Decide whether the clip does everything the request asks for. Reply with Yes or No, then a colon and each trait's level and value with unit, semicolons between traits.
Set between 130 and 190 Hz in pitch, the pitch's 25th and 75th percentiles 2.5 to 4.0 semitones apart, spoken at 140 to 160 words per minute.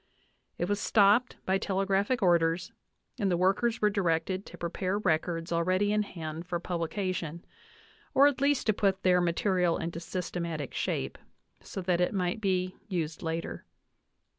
Yes: medium, 185 Hz; average, 2.9 semitones; average, 150 wpm